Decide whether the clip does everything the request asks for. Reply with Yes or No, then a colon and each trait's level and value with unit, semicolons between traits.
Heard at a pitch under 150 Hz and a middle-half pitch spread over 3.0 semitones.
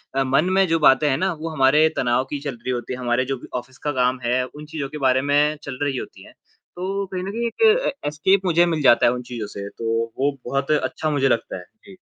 Yes: medium, 140 Hz; average, 3.8 semitones